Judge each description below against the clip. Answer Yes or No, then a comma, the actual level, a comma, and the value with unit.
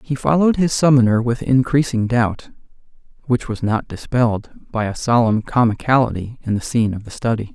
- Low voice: Yes, low, 120 Hz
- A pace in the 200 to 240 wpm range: No, average, 165 wpm